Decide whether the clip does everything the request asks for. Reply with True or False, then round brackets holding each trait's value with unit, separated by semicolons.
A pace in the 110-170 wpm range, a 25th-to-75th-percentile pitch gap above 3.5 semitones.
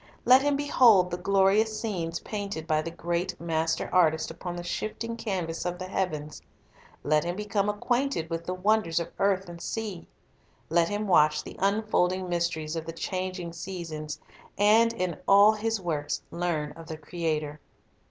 True (160 wpm; 3.9 semitones)